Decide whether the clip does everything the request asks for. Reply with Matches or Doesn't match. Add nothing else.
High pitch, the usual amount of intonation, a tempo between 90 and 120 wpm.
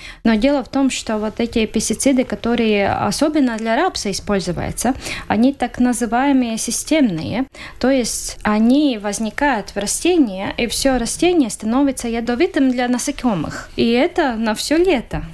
Doesn't match